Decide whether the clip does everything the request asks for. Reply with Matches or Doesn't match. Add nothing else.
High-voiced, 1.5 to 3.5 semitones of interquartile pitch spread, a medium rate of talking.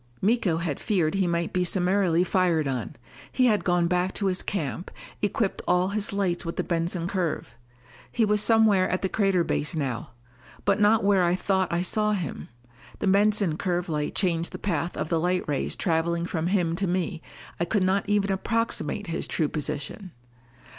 Doesn't match